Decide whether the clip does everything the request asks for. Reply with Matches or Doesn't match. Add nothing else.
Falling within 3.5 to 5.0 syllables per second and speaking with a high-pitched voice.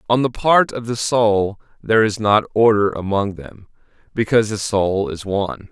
Doesn't match